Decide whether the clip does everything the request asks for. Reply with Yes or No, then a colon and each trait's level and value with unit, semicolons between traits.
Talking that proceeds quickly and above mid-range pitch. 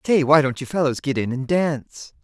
No: fast, 240 wpm; medium, 145 Hz